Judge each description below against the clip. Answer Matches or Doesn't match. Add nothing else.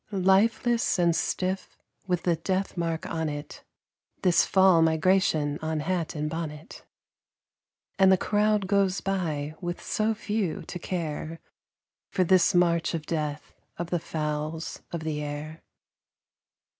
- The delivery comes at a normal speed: Doesn't match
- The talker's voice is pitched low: Doesn't match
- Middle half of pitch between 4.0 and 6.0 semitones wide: Doesn't match